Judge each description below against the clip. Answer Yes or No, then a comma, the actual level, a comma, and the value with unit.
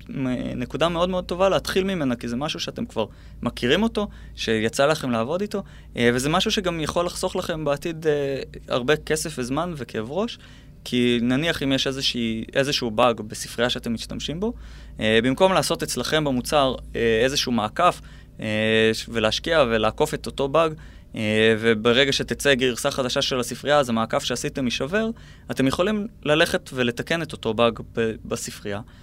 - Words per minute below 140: No, average, 145 wpm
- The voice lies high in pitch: No, low, 135 Hz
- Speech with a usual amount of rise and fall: Yes, average, 4.9 semitones